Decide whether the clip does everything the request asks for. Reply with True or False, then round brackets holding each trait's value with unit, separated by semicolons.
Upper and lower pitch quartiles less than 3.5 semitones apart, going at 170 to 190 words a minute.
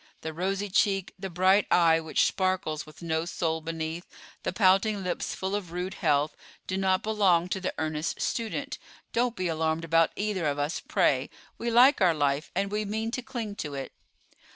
False (4.0 semitones; 185 wpm)